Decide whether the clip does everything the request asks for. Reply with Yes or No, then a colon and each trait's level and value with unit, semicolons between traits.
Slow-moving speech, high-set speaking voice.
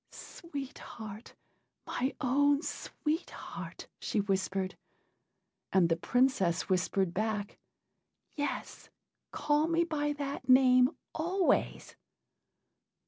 Yes: slow, 90 wpm; very high, 255 Hz